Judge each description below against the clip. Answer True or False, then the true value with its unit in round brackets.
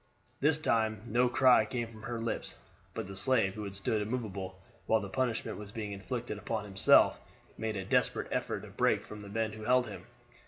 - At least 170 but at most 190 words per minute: False (200 wpm)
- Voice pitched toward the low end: True (110 Hz)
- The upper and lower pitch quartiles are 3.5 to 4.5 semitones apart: False (2.8 semitones)